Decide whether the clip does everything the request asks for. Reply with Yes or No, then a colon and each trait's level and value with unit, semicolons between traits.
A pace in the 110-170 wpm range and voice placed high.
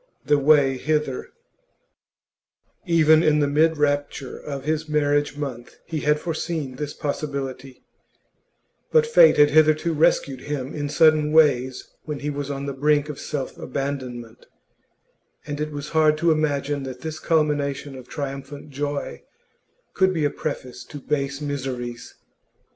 No: average, 140 wpm; medium, 145 Hz